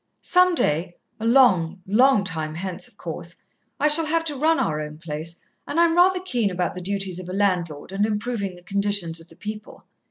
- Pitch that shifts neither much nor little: No, wide, 7.2 semitones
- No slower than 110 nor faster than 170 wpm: No, average, 200 wpm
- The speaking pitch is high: Yes, high, 200 Hz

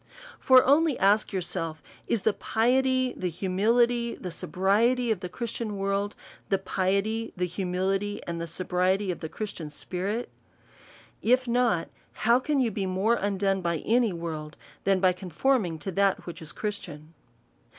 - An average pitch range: Yes, average, 4.3 semitones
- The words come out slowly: No, average, 155 wpm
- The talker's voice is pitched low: No, high, 195 Hz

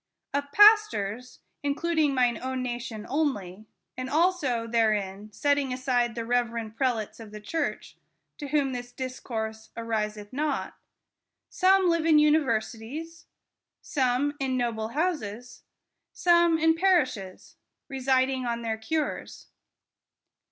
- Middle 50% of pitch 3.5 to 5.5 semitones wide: Yes, average, 5.0 semitones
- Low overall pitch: No, very high, 255 Hz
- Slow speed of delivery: Yes, slow, 120 wpm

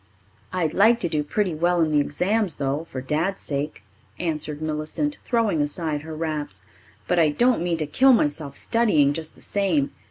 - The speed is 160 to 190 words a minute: Yes, average, 180 wpm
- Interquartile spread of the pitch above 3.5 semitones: Yes, average, 4.3 semitones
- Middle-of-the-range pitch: Yes, medium, 160 Hz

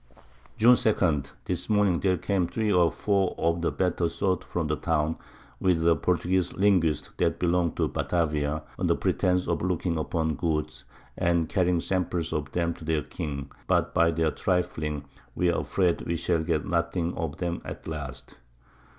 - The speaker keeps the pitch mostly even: Yes, narrow, 2.3 semitones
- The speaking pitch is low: Yes, very low, 85 Hz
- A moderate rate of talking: Yes, average, 170 wpm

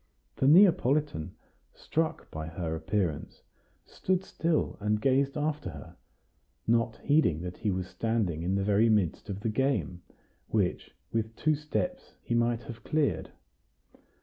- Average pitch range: No, wide, 7.6 semitones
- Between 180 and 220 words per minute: No, average, 140 wpm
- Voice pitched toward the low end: Yes, low, 115 Hz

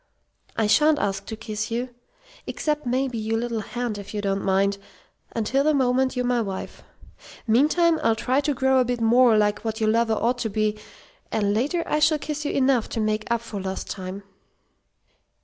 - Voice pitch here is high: Yes, high, 230 Hz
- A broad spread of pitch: No, average, 3.6 semitones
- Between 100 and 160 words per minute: No, average, 190 wpm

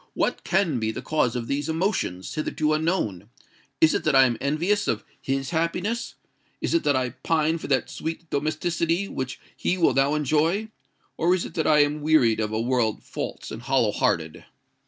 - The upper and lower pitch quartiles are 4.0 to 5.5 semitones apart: Yes, average, 4.8 semitones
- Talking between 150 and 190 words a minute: Yes, average, 185 wpm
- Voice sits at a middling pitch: Yes, medium, 150 Hz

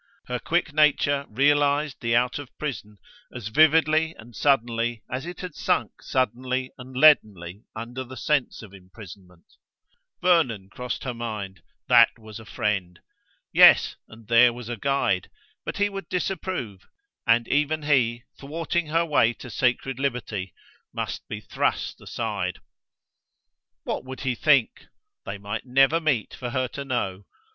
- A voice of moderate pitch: No, low, 125 Hz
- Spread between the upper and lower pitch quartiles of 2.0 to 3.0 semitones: No, average, 4.7 semitones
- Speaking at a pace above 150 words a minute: No, average, 145 wpm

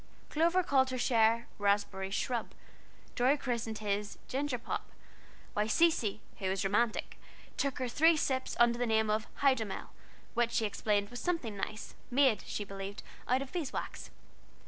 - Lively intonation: No, average, 4.0 semitones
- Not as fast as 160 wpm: Yes, average, 145 wpm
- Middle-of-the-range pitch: No, high, 235 Hz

